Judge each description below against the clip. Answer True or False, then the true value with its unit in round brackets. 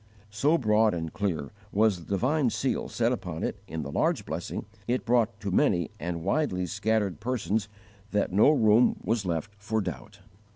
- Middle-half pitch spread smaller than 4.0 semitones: False (4.6 semitones)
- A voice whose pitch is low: True (105 Hz)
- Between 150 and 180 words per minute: True (170 wpm)